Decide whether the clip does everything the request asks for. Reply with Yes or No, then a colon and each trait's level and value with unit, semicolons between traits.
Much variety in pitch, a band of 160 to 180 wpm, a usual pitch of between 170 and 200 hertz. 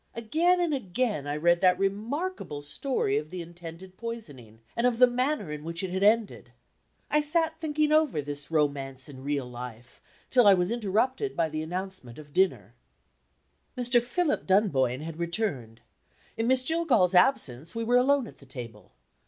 Yes: wide, 9.0 semitones; average, 170 wpm; high, 190 Hz